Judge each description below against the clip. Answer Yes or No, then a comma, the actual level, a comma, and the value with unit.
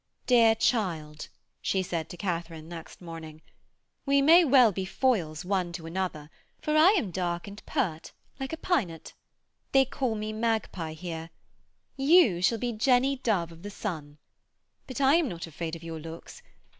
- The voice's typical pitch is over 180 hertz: Yes, high, 190 Hz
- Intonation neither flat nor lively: No, wide, 7.3 semitones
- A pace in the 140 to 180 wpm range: Yes, average, 170 wpm